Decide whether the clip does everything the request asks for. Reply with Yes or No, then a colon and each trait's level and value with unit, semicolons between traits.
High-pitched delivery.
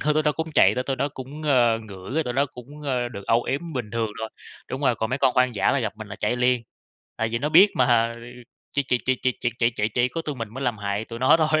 No: low, 125 Hz